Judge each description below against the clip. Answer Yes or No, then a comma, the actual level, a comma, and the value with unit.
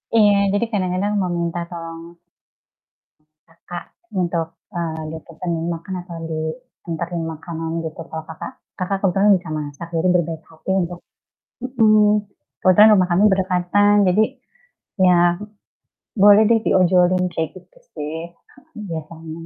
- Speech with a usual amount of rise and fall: Yes, average, 3.3 semitones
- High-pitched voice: No, medium, 175 Hz